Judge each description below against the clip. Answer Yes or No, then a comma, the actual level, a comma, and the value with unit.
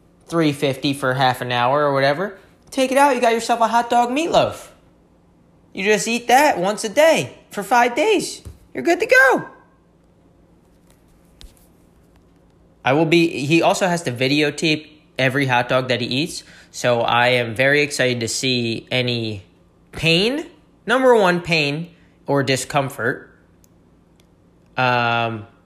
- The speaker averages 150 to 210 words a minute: No, average, 140 wpm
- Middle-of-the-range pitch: Yes, medium, 150 Hz